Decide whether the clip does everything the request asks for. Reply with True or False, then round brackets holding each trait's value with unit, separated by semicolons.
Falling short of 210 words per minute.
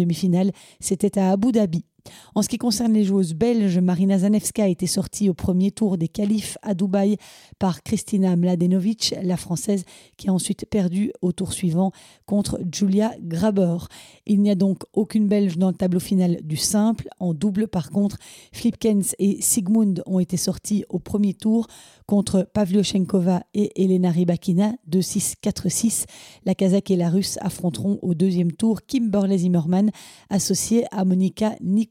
True (160 wpm)